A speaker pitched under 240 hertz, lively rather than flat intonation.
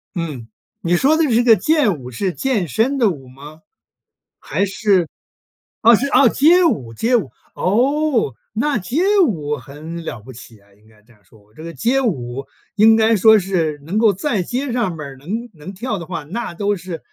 Yes: medium, 185 Hz; wide, 8.2 semitones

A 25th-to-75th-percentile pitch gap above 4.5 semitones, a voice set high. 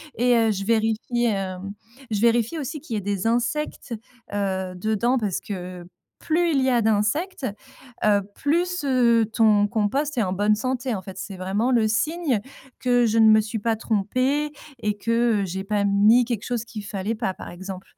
No: average, 3.4 semitones; high, 220 Hz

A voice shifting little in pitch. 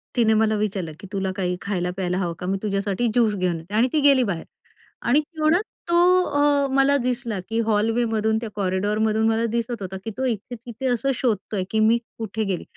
No: average, 3.7 semitones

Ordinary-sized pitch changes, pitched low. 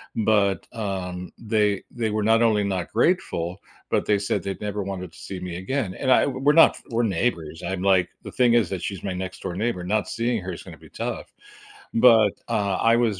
Yes: average, 3.6 semitones; low, 100 Hz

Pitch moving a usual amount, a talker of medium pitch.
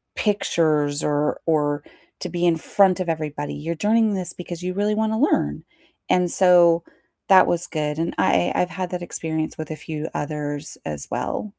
Yes: average, 3.5 semitones; medium, 165 Hz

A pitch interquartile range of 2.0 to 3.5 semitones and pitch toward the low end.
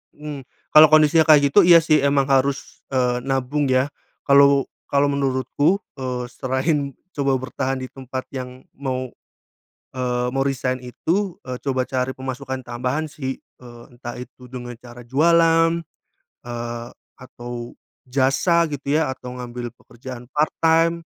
Yes: narrow, 2.4 semitones; low, 130 Hz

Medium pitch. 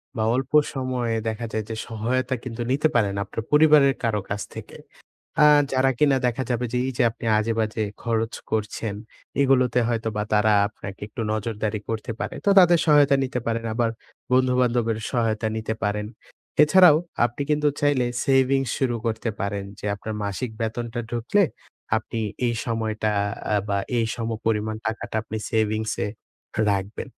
No: low, 115 Hz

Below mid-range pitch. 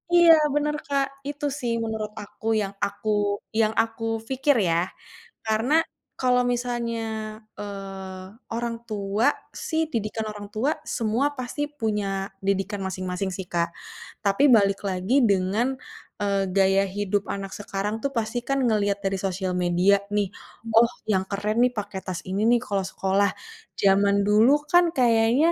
No: high, 210 Hz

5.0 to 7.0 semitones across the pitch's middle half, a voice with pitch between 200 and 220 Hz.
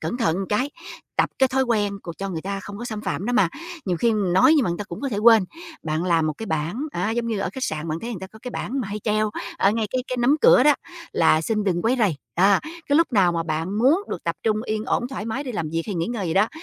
Yes: wide, 5.4 semitones; high, 210 Hz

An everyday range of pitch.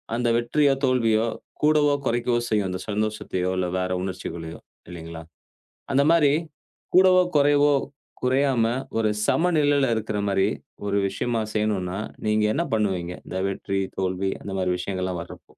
No: wide, 6.7 semitones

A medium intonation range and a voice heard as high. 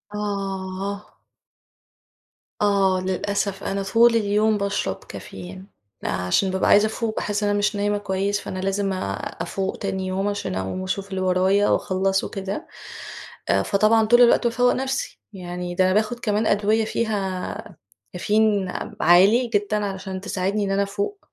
No: narrow, 1.9 semitones; high, 200 Hz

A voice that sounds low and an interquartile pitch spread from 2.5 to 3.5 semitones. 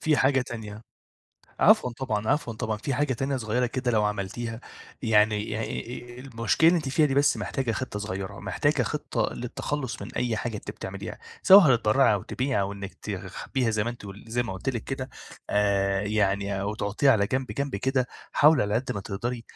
No: low, 115 Hz; average, 4.3 semitones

